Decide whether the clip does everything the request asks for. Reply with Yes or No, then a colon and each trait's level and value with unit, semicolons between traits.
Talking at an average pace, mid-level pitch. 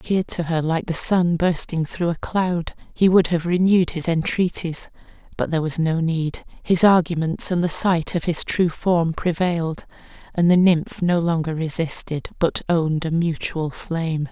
Yes: average, 180 wpm; medium, 170 Hz